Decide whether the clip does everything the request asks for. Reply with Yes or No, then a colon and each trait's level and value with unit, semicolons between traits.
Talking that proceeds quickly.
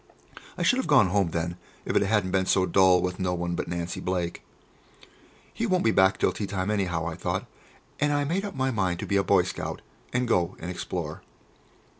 Yes: fast, 215 wpm